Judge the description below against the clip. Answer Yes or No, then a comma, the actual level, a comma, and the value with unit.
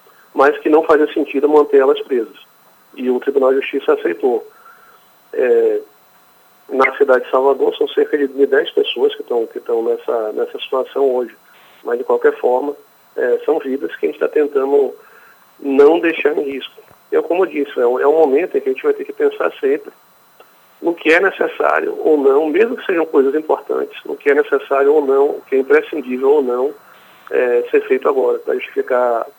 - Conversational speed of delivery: No, fast, 195 wpm